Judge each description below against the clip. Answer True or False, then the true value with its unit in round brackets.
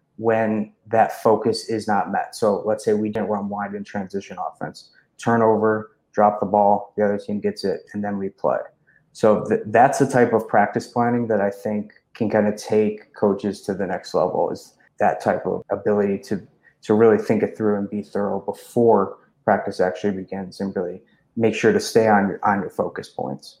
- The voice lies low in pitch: True (105 Hz)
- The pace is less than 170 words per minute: False (200 wpm)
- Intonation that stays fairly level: True (1.5 semitones)